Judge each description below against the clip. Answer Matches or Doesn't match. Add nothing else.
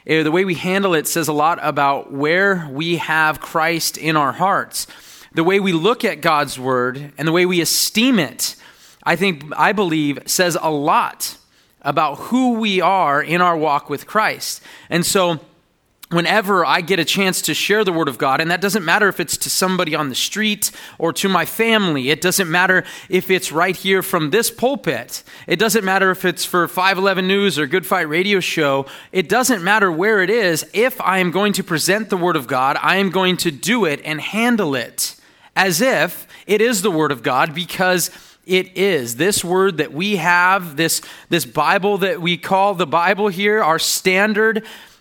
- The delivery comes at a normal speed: Matches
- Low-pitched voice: Doesn't match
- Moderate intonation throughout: Matches